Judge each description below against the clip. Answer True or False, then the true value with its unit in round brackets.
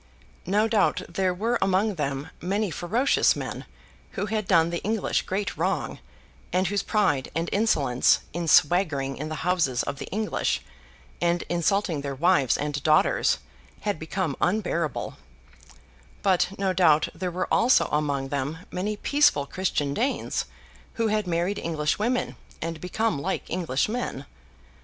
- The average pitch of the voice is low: False (180 Hz)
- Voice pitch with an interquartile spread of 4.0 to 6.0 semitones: True (5.2 semitones)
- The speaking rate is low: False (145 wpm)